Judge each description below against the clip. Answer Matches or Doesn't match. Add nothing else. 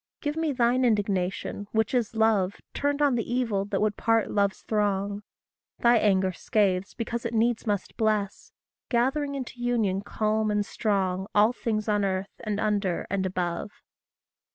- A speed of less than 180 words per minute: Matches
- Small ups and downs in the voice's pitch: Doesn't match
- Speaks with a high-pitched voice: Matches